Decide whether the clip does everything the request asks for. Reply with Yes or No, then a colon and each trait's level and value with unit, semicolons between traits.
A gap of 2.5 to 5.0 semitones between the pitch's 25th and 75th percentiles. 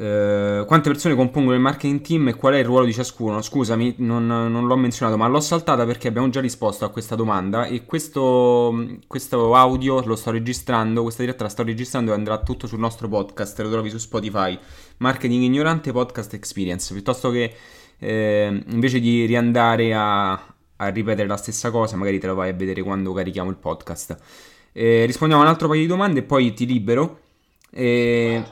Yes: average, 3.1 semitones